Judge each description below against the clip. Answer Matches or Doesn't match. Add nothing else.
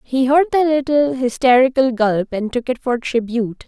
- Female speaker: Matches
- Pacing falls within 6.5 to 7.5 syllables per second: Doesn't match